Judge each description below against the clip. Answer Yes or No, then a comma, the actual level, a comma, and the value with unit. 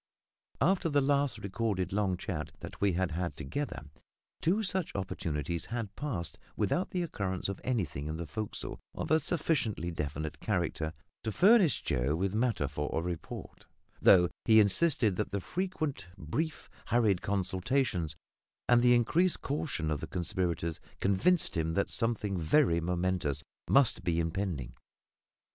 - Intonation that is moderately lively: No, wide, 7.7 semitones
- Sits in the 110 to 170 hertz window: No, low, 100 Hz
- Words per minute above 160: No, average, 145 wpm